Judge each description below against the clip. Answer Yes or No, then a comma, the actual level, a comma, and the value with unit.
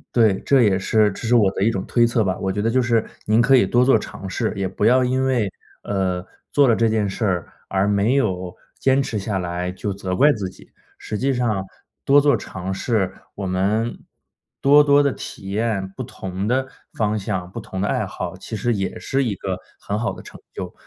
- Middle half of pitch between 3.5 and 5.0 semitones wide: Yes, average, 4.1 semitones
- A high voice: No, low, 105 Hz